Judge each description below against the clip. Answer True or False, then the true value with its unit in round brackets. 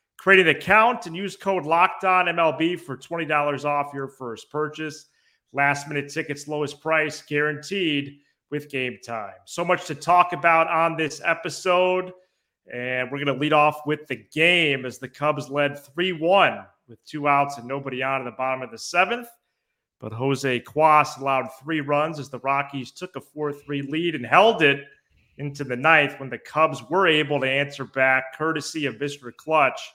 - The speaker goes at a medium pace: True (175 wpm)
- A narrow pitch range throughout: False (3.2 semitones)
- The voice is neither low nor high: True (150 Hz)